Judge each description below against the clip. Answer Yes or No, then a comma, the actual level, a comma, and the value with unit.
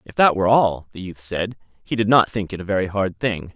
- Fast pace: Yes, fast, 270 wpm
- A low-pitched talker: Yes, low, 100 Hz